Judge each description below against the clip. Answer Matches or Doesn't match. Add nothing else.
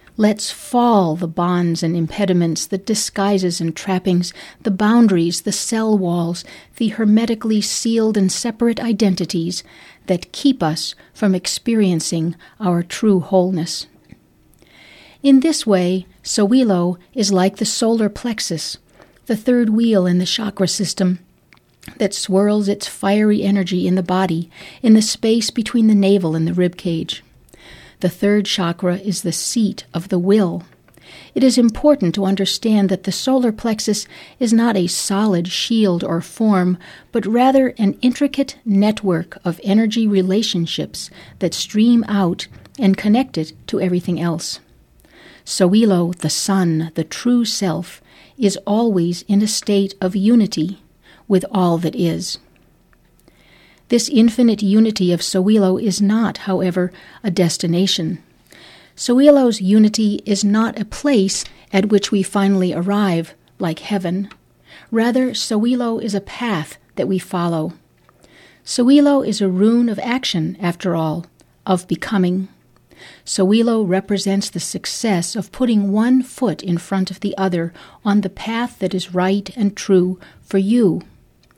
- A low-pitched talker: Doesn't match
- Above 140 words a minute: Doesn't match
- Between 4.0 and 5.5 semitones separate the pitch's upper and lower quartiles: Doesn't match